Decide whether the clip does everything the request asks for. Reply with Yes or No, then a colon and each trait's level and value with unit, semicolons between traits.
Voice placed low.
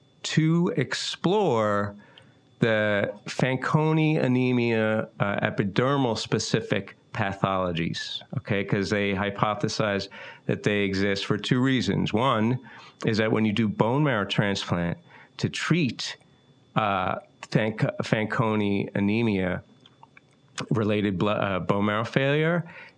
Yes: low, 110 Hz